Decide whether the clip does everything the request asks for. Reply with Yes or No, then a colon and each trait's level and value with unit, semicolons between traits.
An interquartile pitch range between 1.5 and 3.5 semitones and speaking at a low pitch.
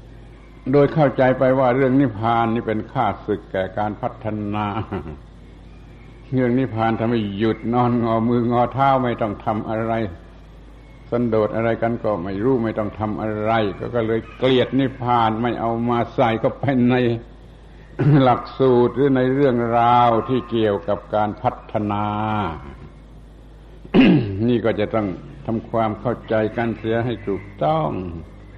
Yes: average, 2.9 semitones; low, 115 Hz